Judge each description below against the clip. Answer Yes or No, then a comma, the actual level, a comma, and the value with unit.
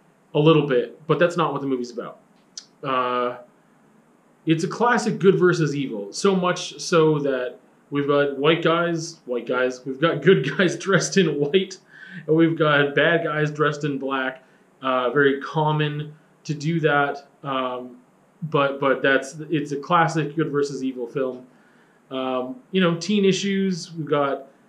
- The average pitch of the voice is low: No, medium, 150 Hz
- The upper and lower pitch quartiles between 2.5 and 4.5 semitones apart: Yes, average, 4.1 semitones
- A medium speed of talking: Yes, average, 160 wpm